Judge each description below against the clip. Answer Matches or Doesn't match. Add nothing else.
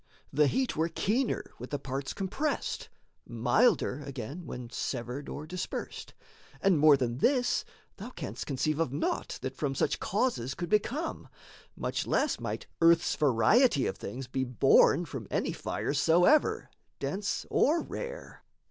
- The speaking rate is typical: Matches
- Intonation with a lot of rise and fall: Matches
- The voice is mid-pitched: Matches